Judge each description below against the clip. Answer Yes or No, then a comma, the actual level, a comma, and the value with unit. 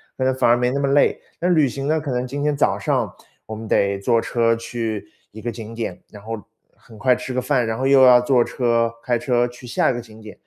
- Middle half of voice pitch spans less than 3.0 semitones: Yes, narrow, 2.6 semitones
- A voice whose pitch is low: Yes, low, 120 Hz